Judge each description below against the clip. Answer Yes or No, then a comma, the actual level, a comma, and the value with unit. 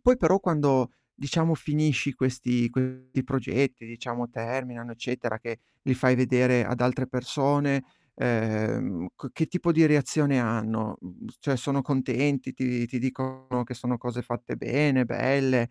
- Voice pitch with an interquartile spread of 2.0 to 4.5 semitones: Yes, narrow, 2.4 semitones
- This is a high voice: No, low, 130 Hz